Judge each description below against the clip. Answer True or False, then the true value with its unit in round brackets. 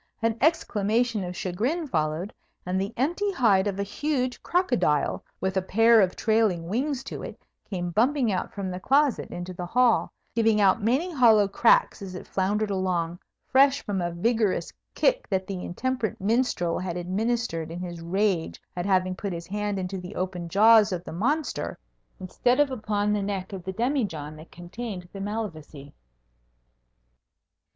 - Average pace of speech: True (165 wpm)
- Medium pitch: False (200 Hz)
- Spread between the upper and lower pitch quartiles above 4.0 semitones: True (4.5 semitones)